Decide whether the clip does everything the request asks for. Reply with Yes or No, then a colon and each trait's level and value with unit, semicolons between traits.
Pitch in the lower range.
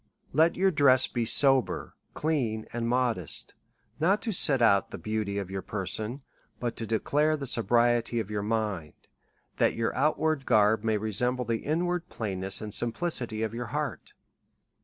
Yes: low, 115 Hz